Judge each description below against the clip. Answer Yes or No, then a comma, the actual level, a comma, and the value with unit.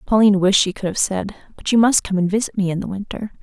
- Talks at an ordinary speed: No, fast, 280 wpm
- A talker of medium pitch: No, high, 200 Hz